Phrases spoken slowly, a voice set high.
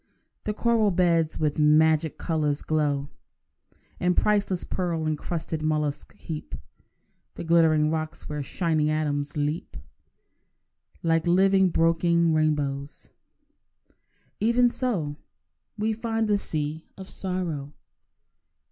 No: slow, 105 wpm; medium, 160 Hz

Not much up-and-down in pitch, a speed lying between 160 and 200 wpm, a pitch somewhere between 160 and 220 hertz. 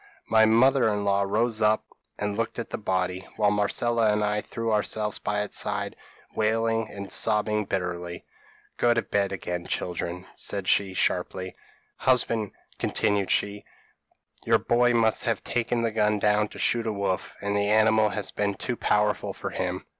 No: narrow, 2.1 semitones; average, 170 wpm; low, 105 Hz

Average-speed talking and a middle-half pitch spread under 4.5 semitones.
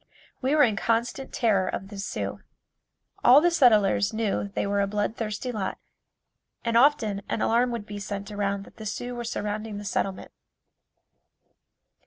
Yes: average, 165 wpm; average, 2.9 semitones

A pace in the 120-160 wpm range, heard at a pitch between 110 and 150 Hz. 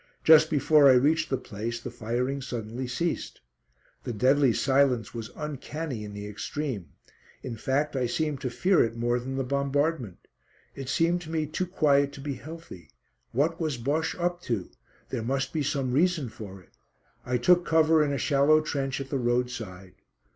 No: average, 175 wpm; low, 135 Hz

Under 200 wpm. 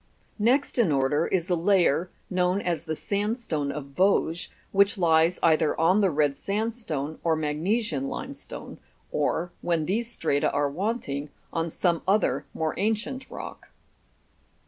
Yes: average, 140 wpm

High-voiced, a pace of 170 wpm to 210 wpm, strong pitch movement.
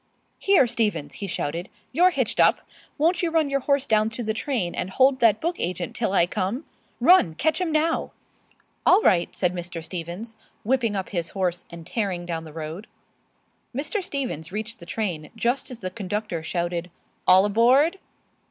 Yes: high, 210 Hz; average, 175 wpm; wide, 7.5 semitones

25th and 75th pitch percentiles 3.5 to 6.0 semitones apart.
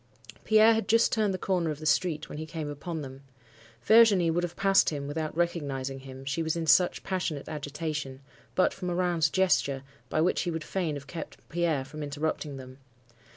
Yes: average, 3.8 semitones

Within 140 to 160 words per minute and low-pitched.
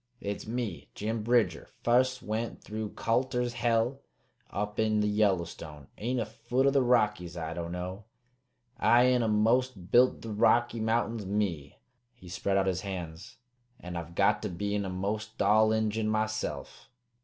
Yes: average, 155 wpm; low, 110 Hz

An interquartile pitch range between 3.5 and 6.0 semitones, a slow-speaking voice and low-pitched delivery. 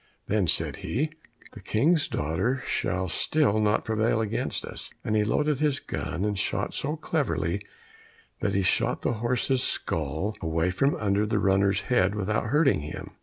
No: average, 5.0 semitones; average, 165 wpm; low, 105 Hz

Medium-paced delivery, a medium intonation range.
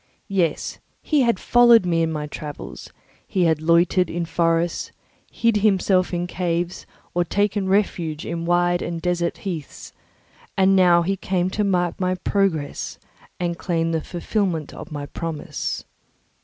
No: average, 145 wpm; narrow, 2.3 semitones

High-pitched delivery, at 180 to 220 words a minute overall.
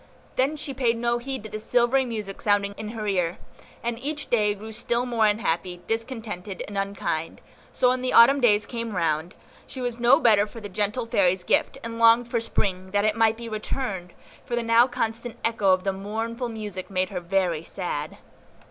Yes: high, 220 Hz; average, 195 wpm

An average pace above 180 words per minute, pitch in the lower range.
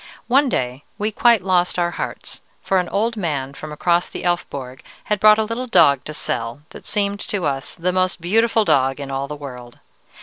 No: average, 200 wpm; medium, 175 Hz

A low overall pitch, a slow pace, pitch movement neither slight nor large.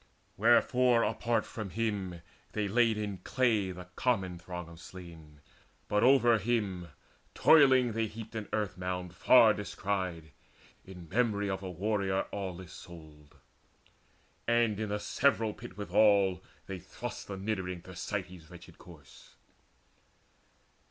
Yes: low, 100 Hz; slow, 125 wpm; average, 3.7 semitones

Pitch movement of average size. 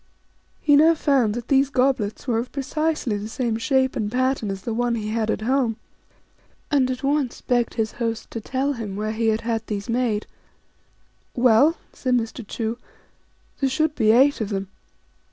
Yes: average, 3.4 semitones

